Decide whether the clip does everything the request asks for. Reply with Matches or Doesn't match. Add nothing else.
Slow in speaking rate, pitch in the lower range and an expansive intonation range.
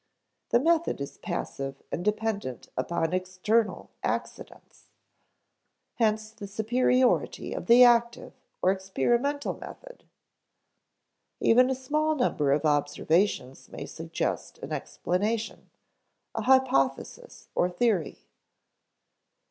Doesn't match